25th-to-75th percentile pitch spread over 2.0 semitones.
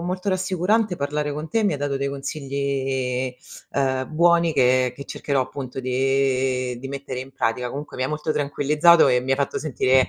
Yes: average, 2.7 semitones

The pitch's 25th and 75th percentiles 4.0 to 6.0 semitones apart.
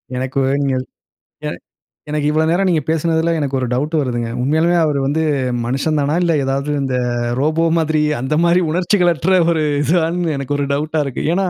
No: average, 3.3 semitones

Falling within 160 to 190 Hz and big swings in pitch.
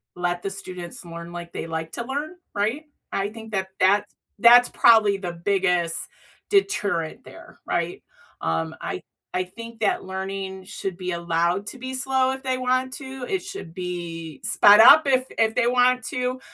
No: high, 200 Hz; wide, 6.2 semitones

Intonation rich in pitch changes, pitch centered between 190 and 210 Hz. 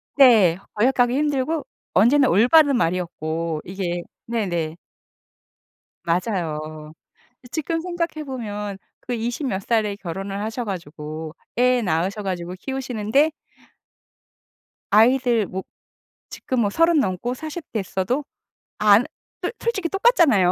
No: wide, 6.5 semitones; high, 220 Hz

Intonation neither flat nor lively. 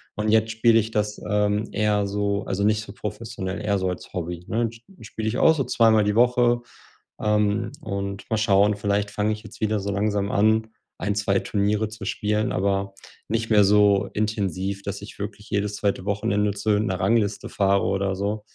No: narrow, 1.5 semitones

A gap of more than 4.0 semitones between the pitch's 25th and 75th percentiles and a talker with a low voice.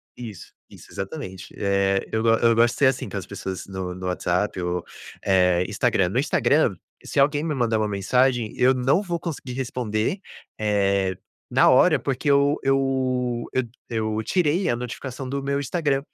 Yes: wide, 5.5 semitones; low, 120 Hz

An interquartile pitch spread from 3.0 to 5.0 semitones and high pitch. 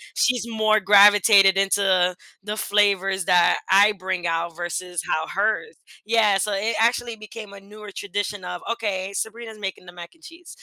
No: narrow, 2.5 semitones; high, 200 Hz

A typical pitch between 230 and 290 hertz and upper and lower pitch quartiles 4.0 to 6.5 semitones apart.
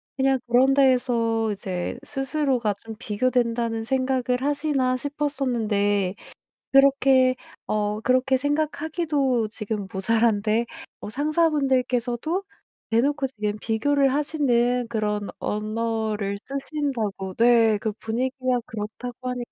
No: high, 245 Hz; average, 3.6 semitones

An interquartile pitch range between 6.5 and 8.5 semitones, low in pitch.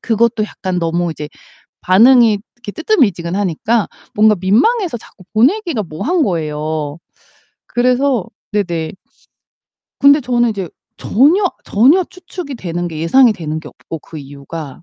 No: wide, 7.3 semitones; high, 210 Hz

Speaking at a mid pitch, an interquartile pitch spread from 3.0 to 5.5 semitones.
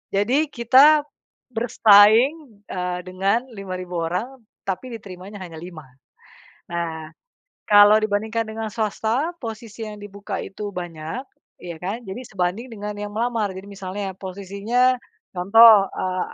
No: high, 205 Hz; average, 3.7 semitones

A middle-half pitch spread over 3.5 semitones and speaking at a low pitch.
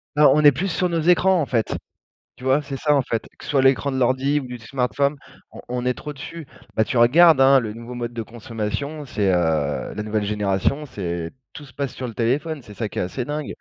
Yes: average, 4.4 semitones; low, 130 Hz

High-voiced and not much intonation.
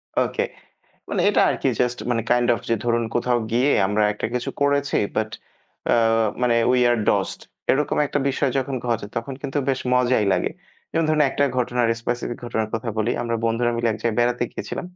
No: low, 120 Hz; narrow, 2.1 semitones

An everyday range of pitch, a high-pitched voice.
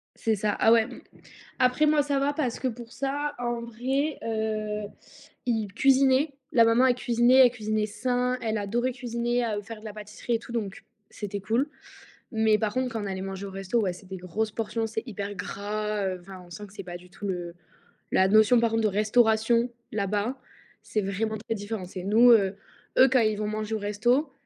Yes: average, 3.0 semitones; high, 220 Hz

